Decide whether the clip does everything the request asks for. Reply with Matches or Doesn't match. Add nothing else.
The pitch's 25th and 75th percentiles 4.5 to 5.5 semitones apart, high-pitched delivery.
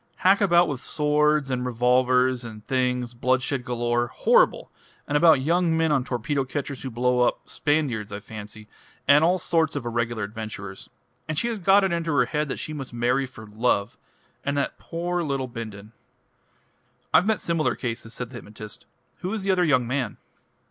Doesn't match